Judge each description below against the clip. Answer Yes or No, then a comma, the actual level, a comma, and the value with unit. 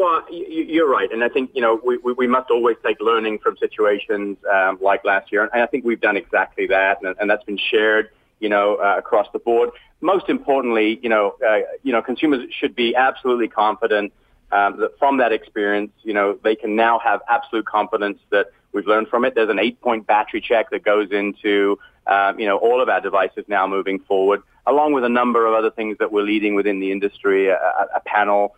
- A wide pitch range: No, average, 3.3 semitones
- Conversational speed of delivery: No, fast, 215 wpm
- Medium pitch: No, low, 110 Hz